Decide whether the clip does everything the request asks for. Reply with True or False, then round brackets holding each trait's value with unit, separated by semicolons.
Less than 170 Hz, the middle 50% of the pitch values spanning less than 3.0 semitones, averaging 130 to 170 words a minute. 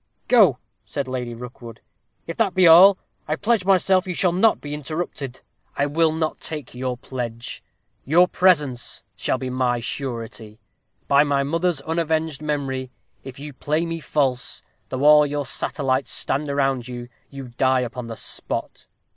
False (140 Hz; 4.2 semitones; 155 wpm)